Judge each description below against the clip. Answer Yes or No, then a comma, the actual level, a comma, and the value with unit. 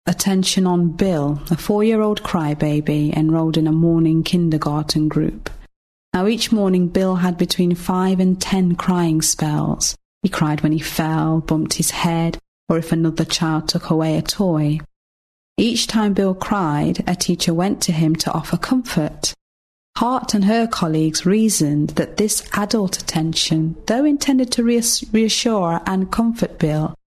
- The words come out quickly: No, average, 150 wpm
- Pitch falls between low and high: Yes, medium, 175 Hz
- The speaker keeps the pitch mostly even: No, average, 4.2 semitones